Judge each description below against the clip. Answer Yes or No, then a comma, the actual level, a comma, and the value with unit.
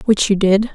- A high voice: Yes, high, 205 Hz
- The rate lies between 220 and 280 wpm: Yes, fast, 240 wpm